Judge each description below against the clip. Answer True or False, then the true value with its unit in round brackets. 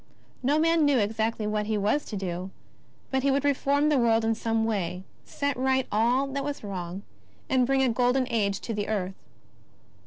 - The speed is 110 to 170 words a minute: False (190 wpm)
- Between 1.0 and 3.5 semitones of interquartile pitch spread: False (4.5 semitones)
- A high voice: True (230 Hz)